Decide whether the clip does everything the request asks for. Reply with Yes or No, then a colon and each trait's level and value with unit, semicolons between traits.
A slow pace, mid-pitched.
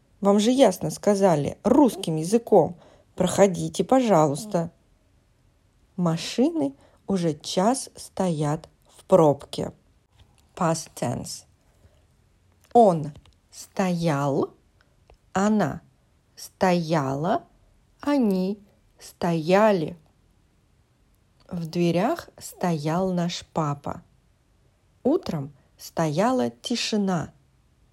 Yes: slow, 65 wpm; medium, 180 Hz